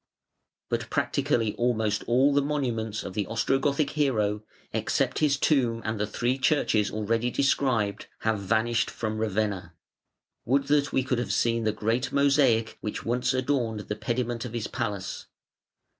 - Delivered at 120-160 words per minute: Yes, average, 150 wpm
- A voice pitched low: Yes, low, 115 Hz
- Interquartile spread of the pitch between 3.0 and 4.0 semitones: Yes, average, 3.7 semitones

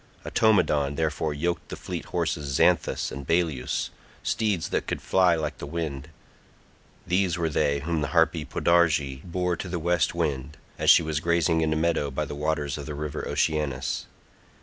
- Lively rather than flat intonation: No, average, 2.9 semitones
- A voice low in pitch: Yes, very low, 80 Hz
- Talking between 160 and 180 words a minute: Yes, average, 170 wpm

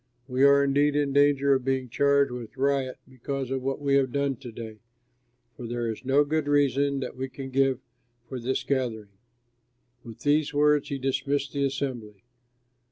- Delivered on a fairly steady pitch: Yes, narrow, 1.7 semitones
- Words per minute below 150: No, average, 175 wpm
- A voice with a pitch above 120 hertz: Yes, low, 135 Hz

